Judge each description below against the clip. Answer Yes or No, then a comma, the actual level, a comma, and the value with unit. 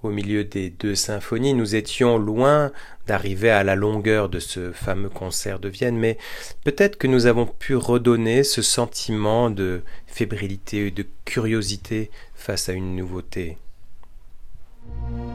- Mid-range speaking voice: No, low, 105 Hz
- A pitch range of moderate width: Yes, average, 3.5 semitones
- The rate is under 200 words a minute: Yes, average, 140 wpm